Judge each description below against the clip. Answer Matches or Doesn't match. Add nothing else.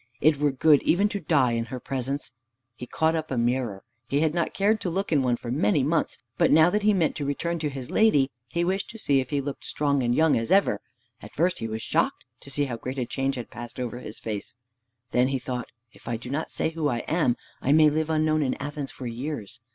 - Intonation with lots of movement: Doesn't match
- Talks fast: Matches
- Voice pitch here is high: Doesn't match